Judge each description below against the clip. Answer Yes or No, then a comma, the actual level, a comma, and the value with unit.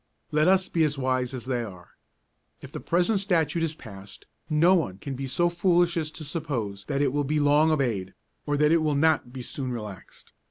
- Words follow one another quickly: Yes, fast, 210 wpm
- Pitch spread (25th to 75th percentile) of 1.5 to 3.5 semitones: No, average, 4.5 semitones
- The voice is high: No, medium, 145 Hz